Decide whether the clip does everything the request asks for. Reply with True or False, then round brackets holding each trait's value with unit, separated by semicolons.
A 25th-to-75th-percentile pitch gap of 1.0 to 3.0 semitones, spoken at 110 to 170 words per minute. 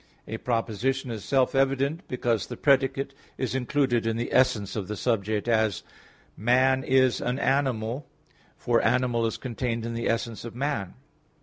True (2.7 semitones; 160 wpm)